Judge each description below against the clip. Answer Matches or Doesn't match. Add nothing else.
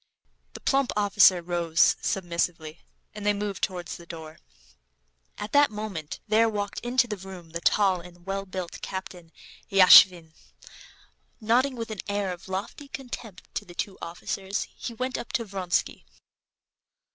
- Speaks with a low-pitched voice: Doesn't match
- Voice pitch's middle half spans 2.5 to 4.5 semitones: Matches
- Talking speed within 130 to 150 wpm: Matches